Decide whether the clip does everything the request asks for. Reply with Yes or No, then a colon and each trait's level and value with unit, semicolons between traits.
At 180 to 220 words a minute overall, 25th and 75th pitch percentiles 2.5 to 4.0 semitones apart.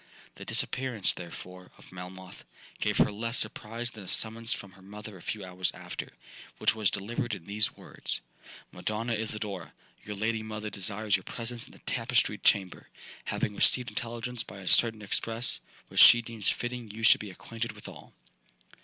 No: average, 165 wpm; average, 2.9 semitones